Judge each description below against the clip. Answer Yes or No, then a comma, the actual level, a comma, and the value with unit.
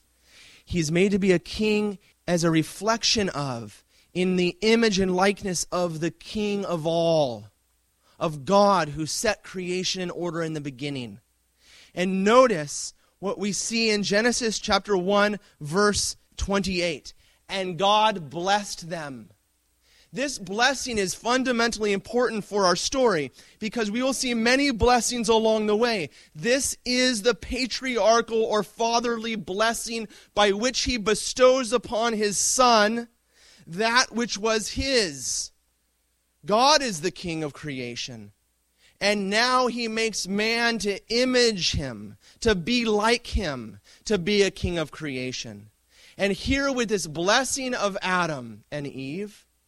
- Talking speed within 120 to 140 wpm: Yes, slow, 135 wpm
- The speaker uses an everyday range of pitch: No, wide, 6.7 semitones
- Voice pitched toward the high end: Yes, high, 200 Hz